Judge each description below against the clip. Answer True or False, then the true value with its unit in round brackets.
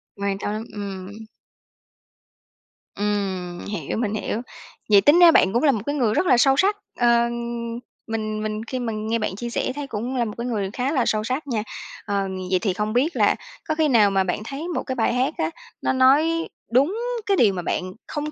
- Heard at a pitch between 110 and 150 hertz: False (230 Hz)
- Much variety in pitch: False (4.5 semitones)